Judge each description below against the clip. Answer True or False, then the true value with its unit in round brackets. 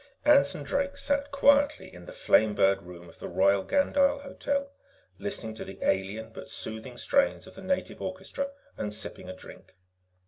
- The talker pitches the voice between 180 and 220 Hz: True (190 Hz)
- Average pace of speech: True (170 wpm)